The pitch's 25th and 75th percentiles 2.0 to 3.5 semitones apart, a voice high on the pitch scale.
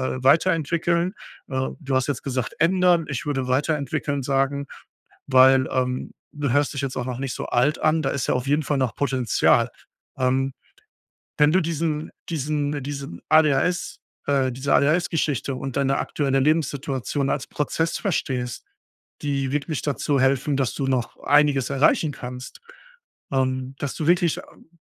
No: narrow, 2.5 semitones; medium, 140 Hz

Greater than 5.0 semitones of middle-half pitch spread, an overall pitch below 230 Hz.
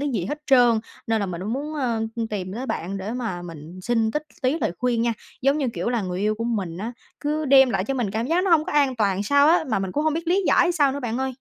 No: wide, 5.4 semitones; high, 240 Hz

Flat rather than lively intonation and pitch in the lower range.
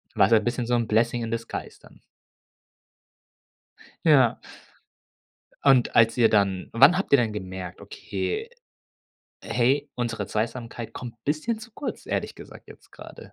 No: average, 3.6 semitones; low, 120 Hz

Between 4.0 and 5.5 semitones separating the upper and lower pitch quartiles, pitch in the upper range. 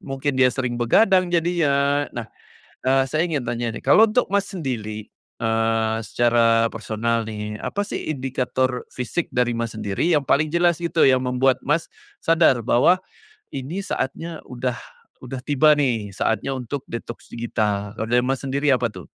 No: average, 4.3 semitones; low, 130 Hz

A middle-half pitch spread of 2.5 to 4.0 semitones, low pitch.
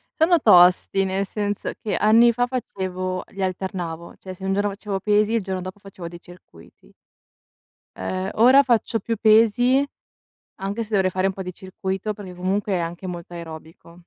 No: average, 2.8 semitones; high, 195 Hz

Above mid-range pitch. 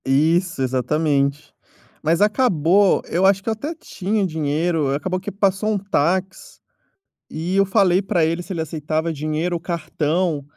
No: medium, 170 Hz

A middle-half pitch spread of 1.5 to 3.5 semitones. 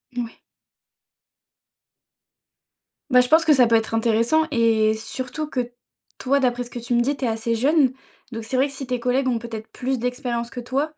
Yes: narrow, 2.5 semitones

